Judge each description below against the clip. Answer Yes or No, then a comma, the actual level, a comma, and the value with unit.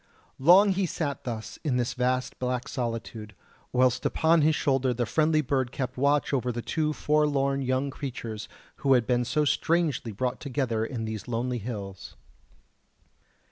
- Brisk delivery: No, average, 155 wpm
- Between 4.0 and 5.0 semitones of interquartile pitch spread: No, average, 3.4 semitones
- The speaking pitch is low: Yes, low, 130 Hz